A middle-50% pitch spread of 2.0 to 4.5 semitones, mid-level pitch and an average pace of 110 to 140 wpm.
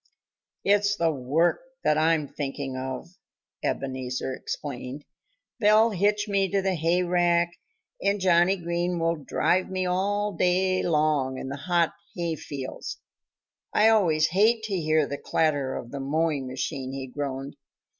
No: average, 4.9 semitones; medium, 165 Hz; slow, 135 wpm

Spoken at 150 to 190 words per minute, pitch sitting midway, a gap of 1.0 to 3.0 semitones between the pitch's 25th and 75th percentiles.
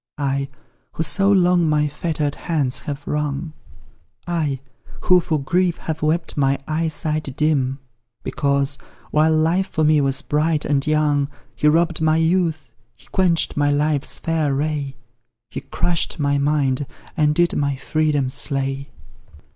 No: average, 140 wpm; medium, 150 Hz; narrow, 2.4 semitones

